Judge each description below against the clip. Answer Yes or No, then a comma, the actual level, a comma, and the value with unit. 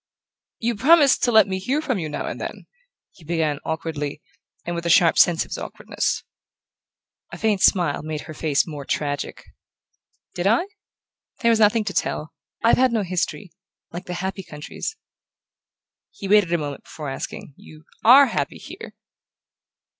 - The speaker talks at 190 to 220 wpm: No, average, 165 wpm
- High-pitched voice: No, medium, 180 Hz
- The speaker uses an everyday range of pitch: No, wide, 6.0 semitones